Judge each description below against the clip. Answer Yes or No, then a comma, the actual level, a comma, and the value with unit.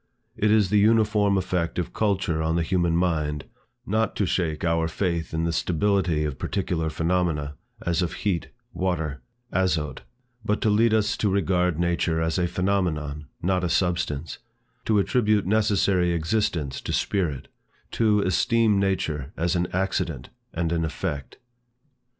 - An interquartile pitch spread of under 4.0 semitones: Yes, average, 3.6 semitones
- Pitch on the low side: Yes, very low, 90 Hz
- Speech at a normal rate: Yes, average, 150 wpm